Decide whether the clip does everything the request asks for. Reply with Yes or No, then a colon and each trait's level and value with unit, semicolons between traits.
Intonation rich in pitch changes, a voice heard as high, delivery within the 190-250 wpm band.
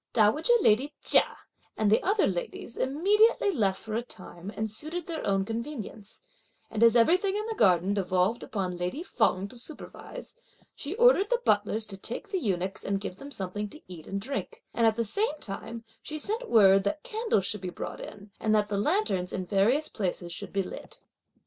Yes: wide, 8.0 semitones; high, 220 Hz; average, 195 wpm